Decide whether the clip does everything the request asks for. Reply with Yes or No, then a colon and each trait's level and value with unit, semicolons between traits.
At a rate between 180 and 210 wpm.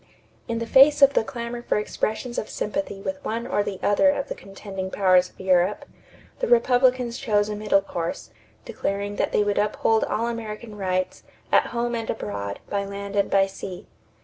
Yes: average, 185 wpm